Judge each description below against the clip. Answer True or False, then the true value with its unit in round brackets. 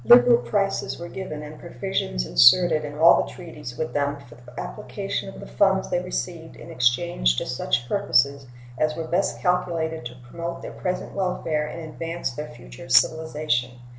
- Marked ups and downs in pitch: True (5.9 semitones)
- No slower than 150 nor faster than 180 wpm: True (170 wpm)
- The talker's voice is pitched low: False (155 Hz)